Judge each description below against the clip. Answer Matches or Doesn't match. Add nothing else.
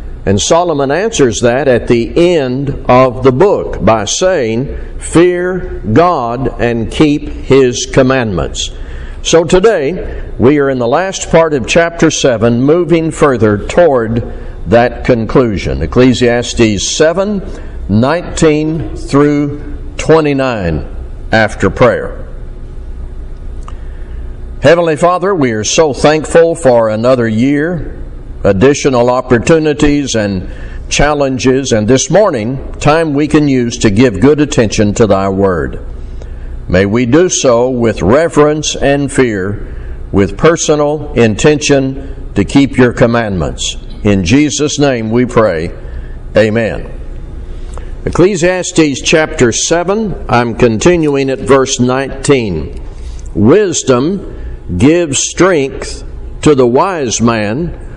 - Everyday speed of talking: Doesn't match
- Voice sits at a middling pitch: Doesn't match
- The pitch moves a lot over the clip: Matches